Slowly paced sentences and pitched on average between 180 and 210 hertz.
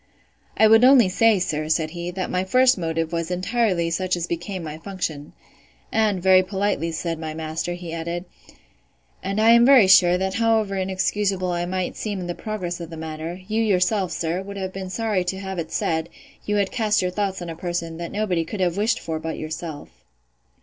No: average, 200 wpm; medium, 185 Hz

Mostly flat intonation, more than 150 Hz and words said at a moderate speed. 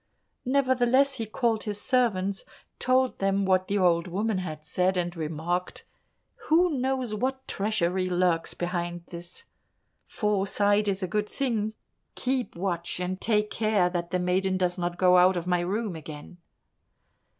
No: average, 3.7 semitones; high, 190 Hz; average, 150 wpm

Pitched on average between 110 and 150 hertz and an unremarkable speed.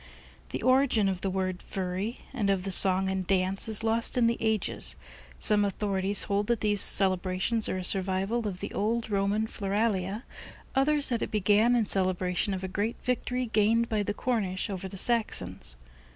No: high, 205 Hz; average, 180 wpm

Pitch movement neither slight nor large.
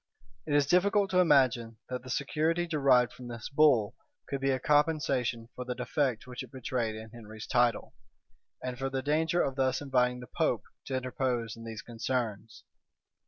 Yes: average, 3.4 semitones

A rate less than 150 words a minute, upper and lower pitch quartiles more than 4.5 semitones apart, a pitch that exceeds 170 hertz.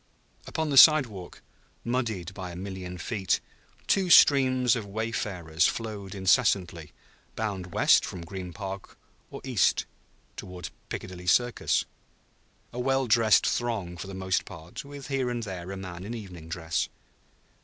No: average, 140 wpm; average, 4.9 semitones; low, 100 Hz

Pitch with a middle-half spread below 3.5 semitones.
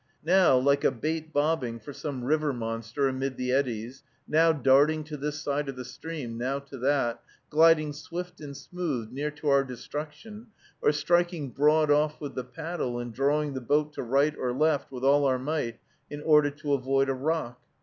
Yes: average, 2.9 semitones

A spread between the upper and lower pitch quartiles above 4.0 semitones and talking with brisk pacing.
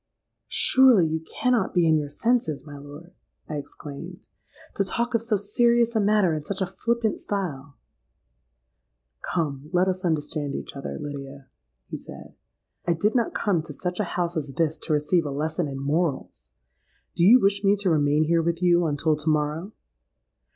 No: average, 5.2 semitones; average, 170 wpm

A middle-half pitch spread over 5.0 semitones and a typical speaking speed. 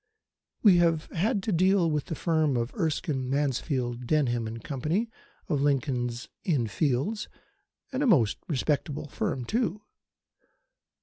No: wide, 5.4 semitones; slow, 130 wpm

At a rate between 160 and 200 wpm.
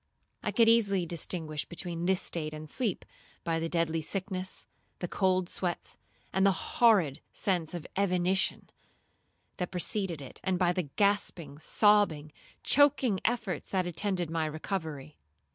No: average, 140 wpm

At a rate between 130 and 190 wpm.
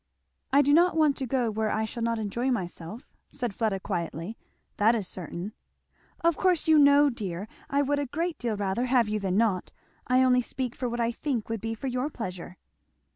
No: fast, 205 wpm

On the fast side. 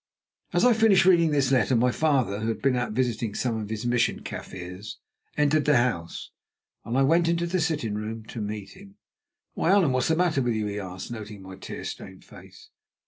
Yes: fast, 210 wpm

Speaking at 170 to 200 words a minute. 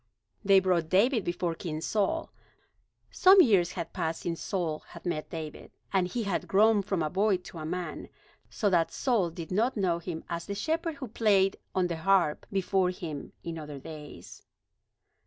Yes: average, 180 wpm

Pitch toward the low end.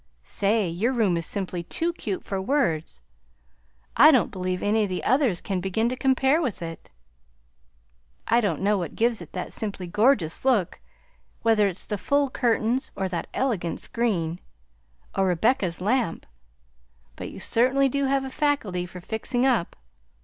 No: high, 210 Hz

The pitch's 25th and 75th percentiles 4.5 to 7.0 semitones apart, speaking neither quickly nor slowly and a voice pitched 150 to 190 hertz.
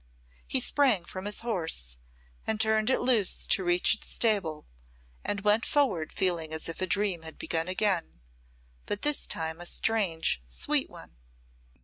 Yes: average, 5.0 semitones; average, 155 wpm; medium, 185 Hz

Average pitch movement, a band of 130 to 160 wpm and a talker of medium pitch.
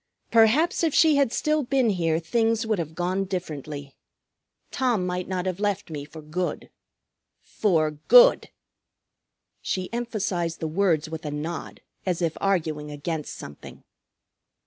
No: wide, 5.9 semitones; average, 140 wpm; medium, 180 Hz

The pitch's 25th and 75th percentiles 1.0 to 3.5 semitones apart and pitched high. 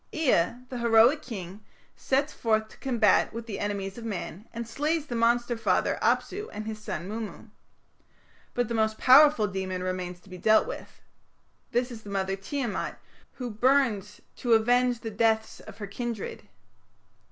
Yes: average, 3.1 semitones; high, 225 Hz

